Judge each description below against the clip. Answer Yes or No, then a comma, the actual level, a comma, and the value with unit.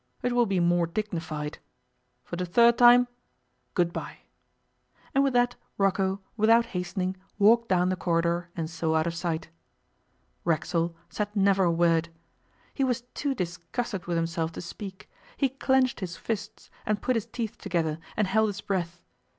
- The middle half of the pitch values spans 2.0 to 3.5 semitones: No, average, 5.0 semitones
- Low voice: No, medium, 185 Hz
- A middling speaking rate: Yes, average, 160 wpm